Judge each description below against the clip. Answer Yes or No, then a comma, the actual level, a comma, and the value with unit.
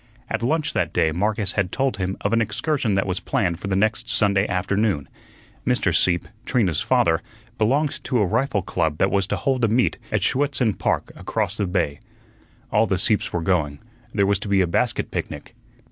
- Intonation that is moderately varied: Yes, average, 3.8 semitones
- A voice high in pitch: No, low, 100 Hz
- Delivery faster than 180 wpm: Yes, average, 195 wpm